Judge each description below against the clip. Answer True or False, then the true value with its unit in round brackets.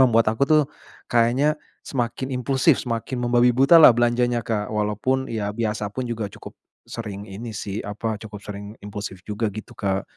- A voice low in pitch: True (115 Hz)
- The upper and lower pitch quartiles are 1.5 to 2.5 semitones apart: False (2.9 semitones)